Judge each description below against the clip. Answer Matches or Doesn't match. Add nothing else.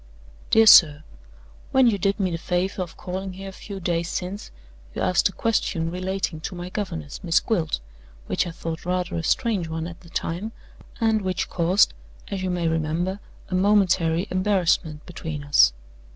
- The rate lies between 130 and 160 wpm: Doesn't match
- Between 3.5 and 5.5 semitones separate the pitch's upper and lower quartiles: Doesn't match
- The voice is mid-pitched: Matches